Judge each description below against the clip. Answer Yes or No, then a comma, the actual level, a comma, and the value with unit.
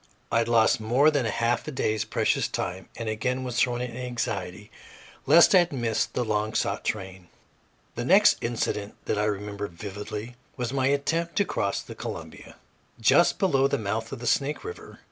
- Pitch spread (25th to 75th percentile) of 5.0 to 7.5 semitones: No, average, 4.0 semitones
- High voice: No, low, 120 Hz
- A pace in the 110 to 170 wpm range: No, average, 180 wpm